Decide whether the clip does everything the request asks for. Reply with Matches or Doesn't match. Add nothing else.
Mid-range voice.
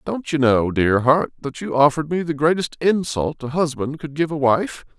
Matches